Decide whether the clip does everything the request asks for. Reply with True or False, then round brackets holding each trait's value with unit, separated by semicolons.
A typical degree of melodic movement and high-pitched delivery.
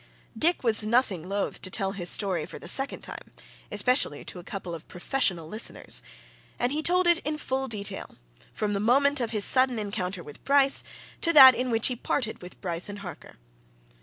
False (5.8 semitones; 220 Hz)